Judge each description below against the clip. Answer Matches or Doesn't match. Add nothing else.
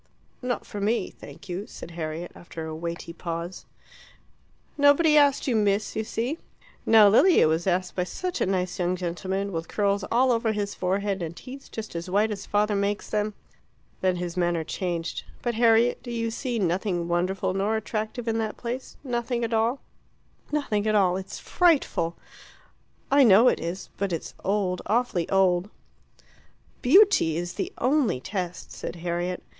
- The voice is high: Matches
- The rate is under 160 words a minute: Doesn't match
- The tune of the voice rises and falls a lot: Doesn't match